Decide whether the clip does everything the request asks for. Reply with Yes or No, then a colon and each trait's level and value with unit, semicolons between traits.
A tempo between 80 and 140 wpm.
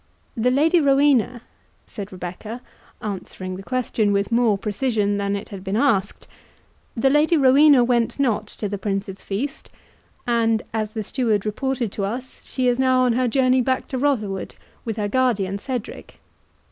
No: average, 160 wpm